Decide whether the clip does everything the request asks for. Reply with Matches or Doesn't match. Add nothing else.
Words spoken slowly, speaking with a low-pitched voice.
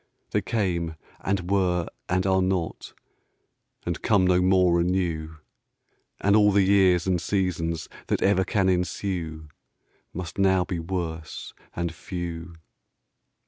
Matches